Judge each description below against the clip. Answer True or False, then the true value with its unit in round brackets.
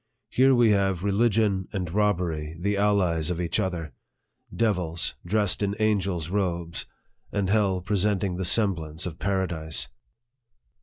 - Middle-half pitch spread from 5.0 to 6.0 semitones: False (3.1 semitones)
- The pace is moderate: False (125 wpm)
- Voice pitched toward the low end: True (95 Hz)